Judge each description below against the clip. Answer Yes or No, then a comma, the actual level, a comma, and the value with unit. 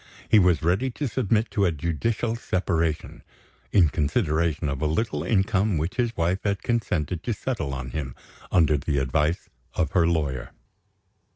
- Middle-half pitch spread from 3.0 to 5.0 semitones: No, wide, 5.5 semitones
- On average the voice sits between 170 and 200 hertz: No, very low, 85 Hz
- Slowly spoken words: No, average, 160 wpm